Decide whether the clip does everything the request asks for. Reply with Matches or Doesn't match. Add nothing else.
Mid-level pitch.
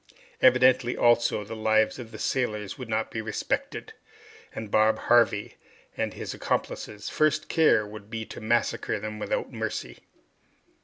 Doesn't match